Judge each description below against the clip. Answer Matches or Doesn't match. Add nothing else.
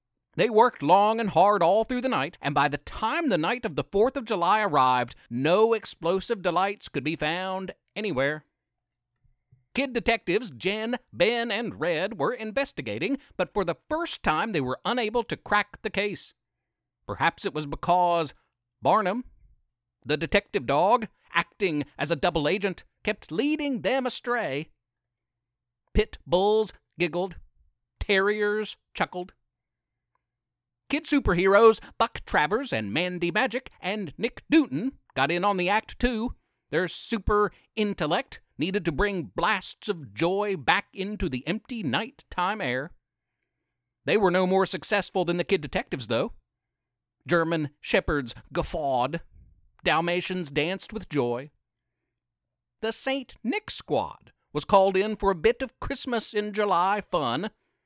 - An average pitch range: Doesn't match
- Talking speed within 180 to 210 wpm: Doesn't match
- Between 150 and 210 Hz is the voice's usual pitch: Matches